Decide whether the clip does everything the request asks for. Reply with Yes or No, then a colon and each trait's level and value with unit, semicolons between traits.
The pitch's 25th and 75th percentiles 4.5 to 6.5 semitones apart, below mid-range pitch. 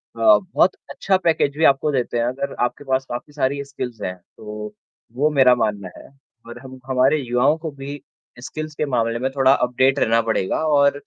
No: average, 2.9 semitones; low, 130 Hz